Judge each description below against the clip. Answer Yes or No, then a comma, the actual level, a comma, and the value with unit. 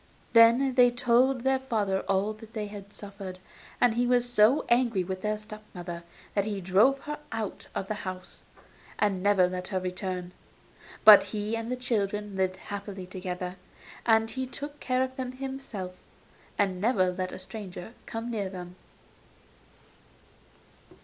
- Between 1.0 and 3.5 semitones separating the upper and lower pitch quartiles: No, average, 4.3 semitones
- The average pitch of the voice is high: Yes, high, 210 Hz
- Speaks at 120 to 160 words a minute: Yes, average, 155 wpm